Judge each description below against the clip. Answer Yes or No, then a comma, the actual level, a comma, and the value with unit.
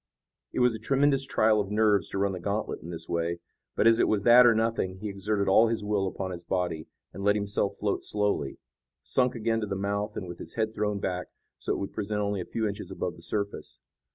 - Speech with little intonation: Yes, narrow, 2.2 semitones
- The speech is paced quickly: Yes, fast, 240 wpm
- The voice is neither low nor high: No, low, 105 Hz